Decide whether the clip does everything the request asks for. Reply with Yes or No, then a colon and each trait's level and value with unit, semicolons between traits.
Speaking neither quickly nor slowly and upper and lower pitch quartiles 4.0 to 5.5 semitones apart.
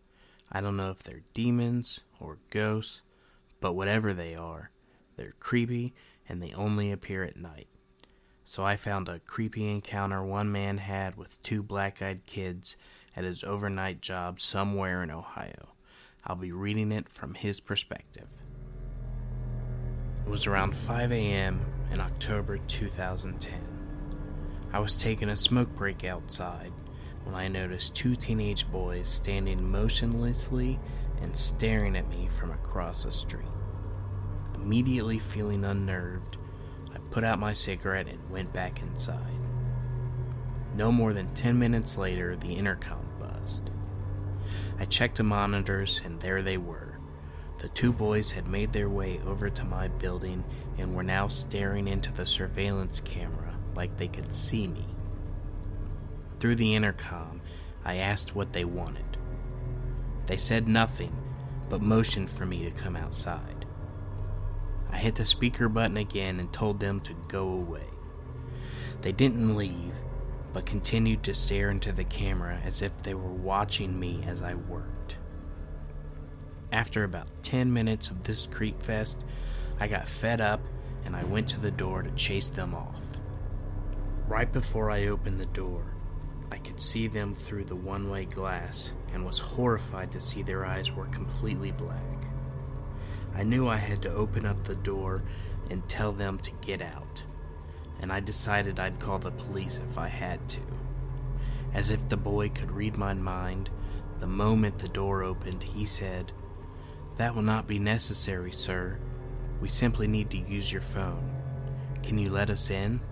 No: average, 150 wpm; average, 3.3 semitones